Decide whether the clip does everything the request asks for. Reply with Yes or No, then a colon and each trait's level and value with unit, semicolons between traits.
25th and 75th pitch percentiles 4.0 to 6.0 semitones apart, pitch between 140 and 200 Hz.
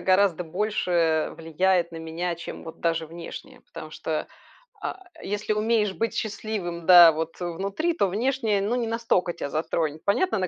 Yes: average, 4.3 semitones; medium, 185 Hz